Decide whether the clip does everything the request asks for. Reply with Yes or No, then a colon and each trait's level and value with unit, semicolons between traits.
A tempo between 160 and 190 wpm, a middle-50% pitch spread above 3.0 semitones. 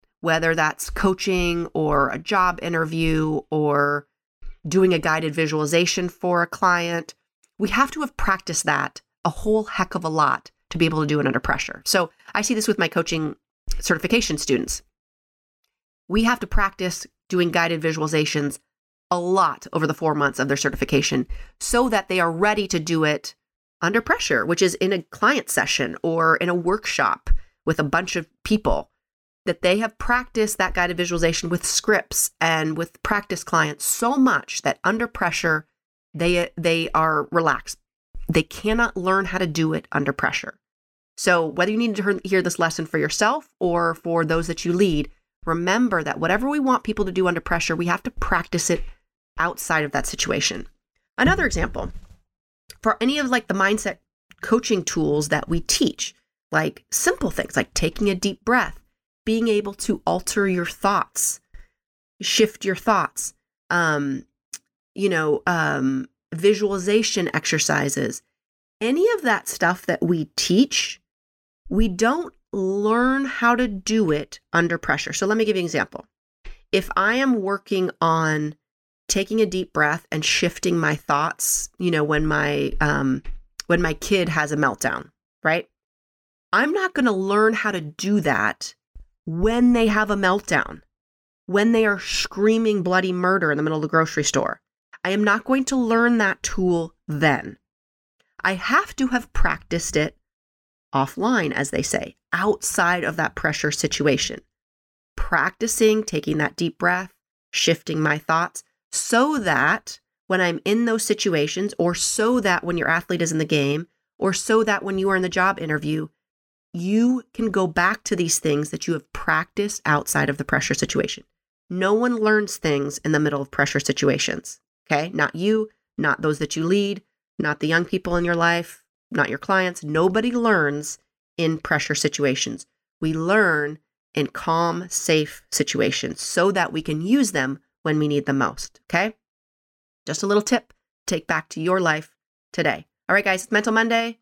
Yes: average, 170 wpm; average, 5.0 semitones